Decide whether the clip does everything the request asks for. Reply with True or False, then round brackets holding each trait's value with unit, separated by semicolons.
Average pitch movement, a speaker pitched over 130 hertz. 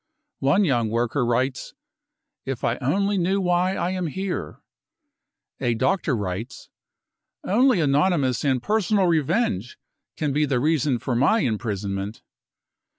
False (7.4 semitones; 140 Hz)